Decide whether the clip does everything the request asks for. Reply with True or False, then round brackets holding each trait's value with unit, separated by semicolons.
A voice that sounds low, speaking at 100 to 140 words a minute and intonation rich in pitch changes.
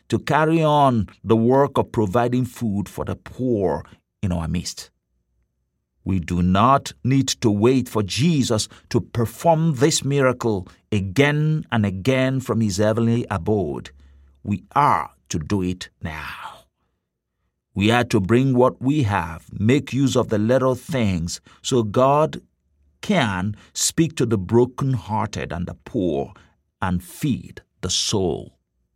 True (110 Hz; 135 wpm; 6.1 semitones)